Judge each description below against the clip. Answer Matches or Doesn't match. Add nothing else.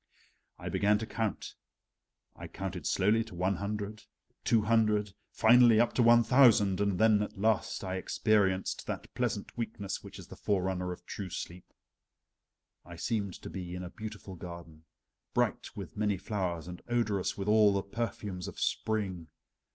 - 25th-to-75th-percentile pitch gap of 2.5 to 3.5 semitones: Matches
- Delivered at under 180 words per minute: Matches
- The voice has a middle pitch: Doesn't match